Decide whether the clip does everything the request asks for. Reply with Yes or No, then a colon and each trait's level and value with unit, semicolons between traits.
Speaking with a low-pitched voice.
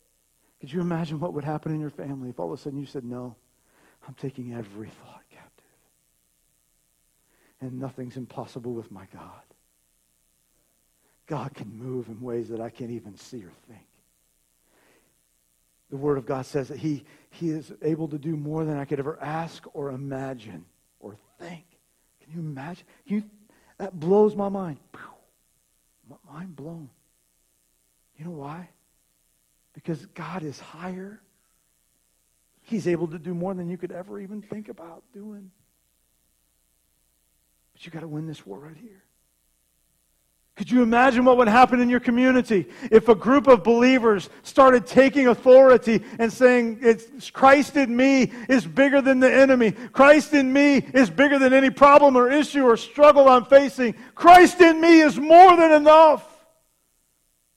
No: medium, 165 Hz